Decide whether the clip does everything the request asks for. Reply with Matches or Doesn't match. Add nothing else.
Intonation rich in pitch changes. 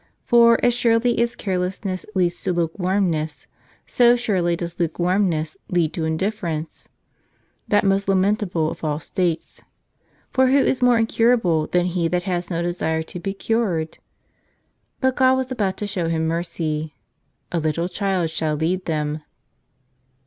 Doesn't match